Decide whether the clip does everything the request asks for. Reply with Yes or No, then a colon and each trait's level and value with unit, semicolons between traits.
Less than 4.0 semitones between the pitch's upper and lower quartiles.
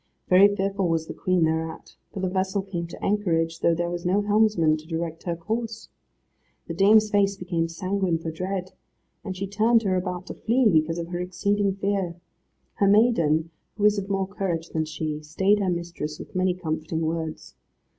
Yes: average, 3.3 semitones